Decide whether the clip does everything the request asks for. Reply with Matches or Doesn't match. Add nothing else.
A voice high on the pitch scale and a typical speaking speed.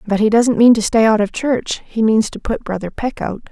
Doesn't match